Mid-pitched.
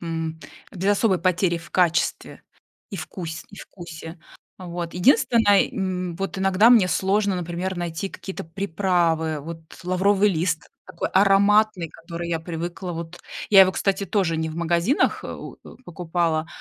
Yes: medium, 180 Hz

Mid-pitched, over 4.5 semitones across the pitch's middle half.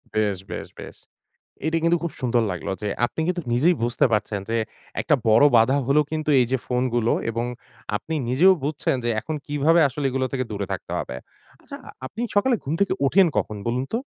No: low, 130 Hz; average, 5.3 semitones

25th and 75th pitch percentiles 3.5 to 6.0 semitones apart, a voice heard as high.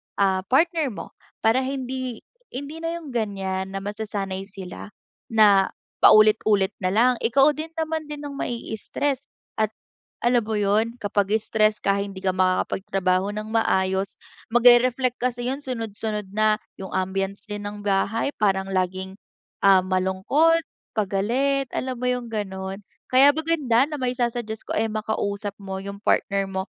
Yes: average, 4.6 semitones; high, 215 Hz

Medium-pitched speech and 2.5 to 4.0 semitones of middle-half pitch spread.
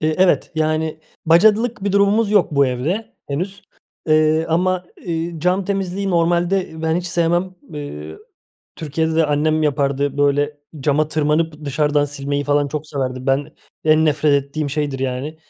Yes: medium, 155 Hz; average, 3.3 semitones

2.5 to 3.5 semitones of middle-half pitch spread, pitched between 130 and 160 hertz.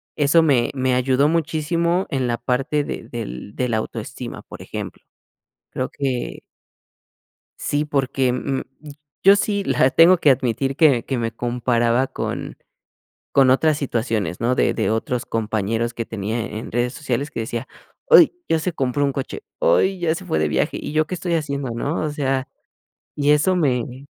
No: average, 4.2 semitones; low, 135 Hz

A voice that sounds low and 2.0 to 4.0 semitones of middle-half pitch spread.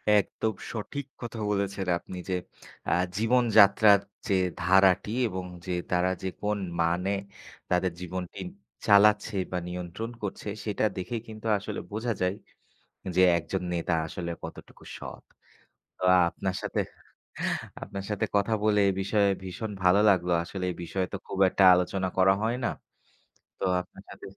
Yes: very low, 95 Hz; narrow, 2.5 semitones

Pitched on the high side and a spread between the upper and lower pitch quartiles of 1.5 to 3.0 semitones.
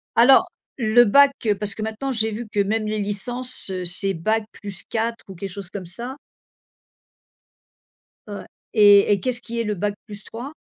Yes: high, 215 Hz; average, 2.7 semitones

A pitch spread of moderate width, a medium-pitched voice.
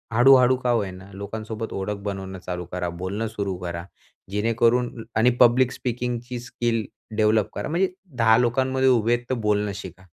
No: average, 3.5 semitones; low, 110 Hz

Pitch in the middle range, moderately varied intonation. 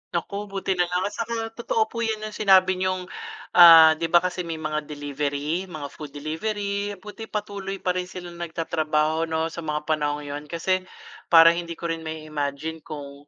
Yes: medium, 165 Hz; average, 3.5 semitones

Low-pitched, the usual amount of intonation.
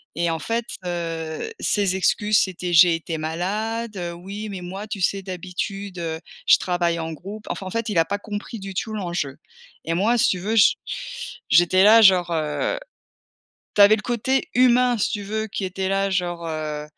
No: high, 190 Hz; average, 3.6 semitones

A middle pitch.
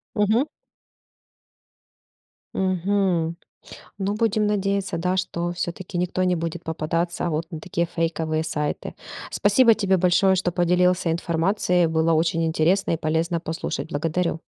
Yes: medium, 175 Hz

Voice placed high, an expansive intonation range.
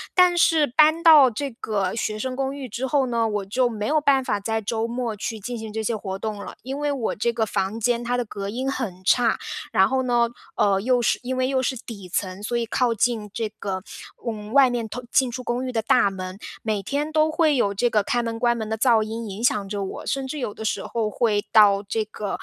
No: high, 230 Hz; average, 3.6 semitones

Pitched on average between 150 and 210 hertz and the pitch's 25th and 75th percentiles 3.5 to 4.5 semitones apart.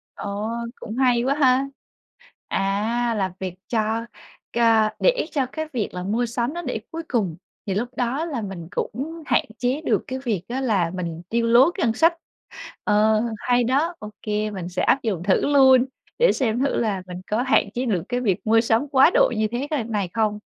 No: high, 235 Hz; average, 4.0 semitones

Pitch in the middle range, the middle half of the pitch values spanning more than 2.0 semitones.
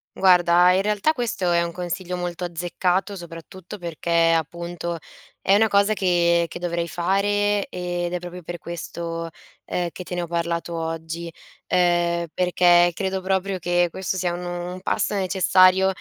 No: medium, 175 Hz; narrow, 1.6 semitones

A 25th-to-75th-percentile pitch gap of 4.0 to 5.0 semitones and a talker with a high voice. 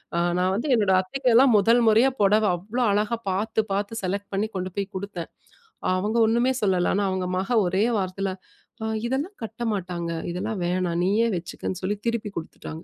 No: average, 3.4 semitones; high, 200 Hz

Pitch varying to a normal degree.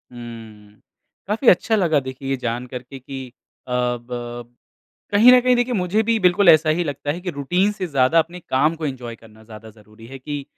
No: wide, 6.7 semitones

